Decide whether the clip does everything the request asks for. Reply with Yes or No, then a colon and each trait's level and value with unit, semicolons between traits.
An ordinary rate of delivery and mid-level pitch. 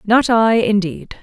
No: average, 145 wpm; high, 210 Hz